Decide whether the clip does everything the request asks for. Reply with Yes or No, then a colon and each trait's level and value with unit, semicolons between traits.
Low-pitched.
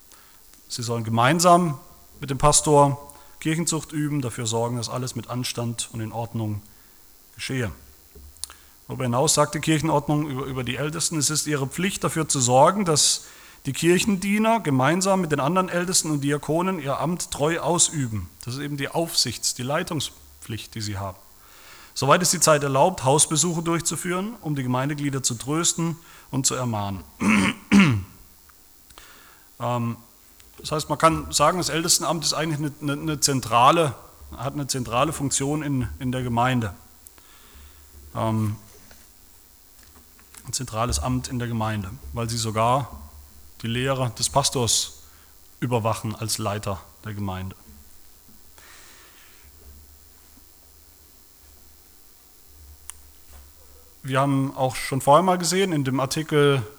Yes: low, 125 Hz